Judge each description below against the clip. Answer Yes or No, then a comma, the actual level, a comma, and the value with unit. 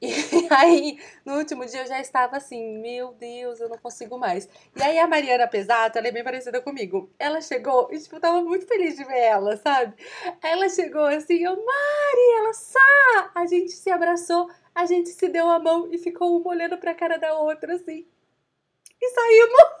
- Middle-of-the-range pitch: No, very high, 320 Hz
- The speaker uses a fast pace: Yes, fast, 200 wpm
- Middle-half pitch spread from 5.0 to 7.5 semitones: Yes, wide, 5.5 semitones